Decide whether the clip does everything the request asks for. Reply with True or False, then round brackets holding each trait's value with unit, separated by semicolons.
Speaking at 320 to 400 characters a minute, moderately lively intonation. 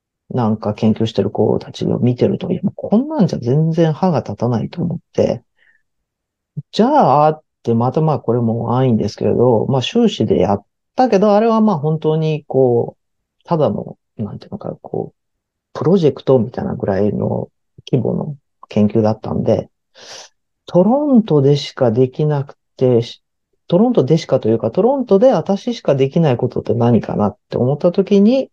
False (340 characters per minute; 8.2 semitones)